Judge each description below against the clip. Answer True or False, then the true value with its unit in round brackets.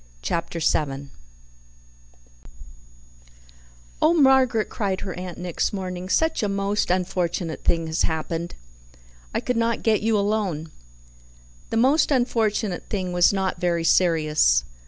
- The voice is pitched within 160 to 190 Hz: True (185 Hz)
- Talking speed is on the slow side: True (120 wpm)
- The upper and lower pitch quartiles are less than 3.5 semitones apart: False (4.5 semitones)